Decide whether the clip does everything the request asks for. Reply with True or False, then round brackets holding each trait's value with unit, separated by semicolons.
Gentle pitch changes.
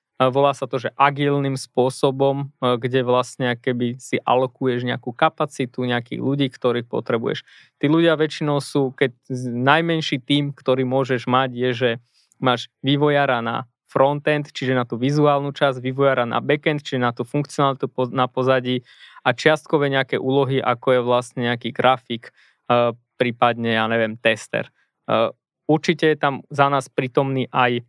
True (2.3 semitones)